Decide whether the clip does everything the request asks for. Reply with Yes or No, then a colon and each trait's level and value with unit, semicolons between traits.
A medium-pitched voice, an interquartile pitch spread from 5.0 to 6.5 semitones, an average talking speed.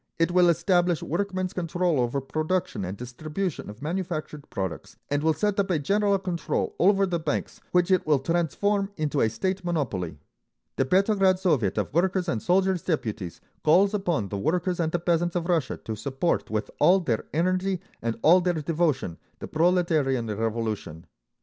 Yes: medium, 170 Hz; wide, 5.5 semitones; average, 170 wpm